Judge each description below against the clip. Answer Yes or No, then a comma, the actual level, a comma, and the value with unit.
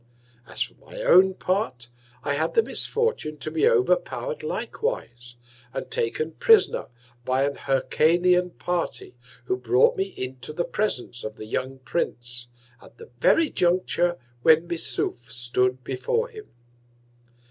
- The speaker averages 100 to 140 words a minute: Yes, slow, 135 wpm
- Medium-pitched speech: Yes, medium, 160 Hz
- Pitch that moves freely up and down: Yes, wide, 8.1 semitones